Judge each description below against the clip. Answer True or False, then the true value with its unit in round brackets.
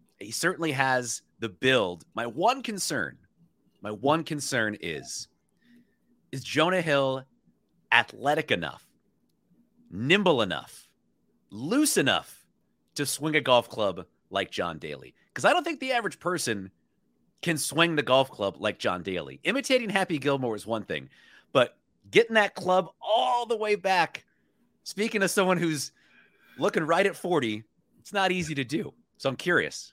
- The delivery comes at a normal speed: True (150 wpm)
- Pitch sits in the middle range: True (160 Hz)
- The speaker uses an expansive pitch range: True (7.4 semitones)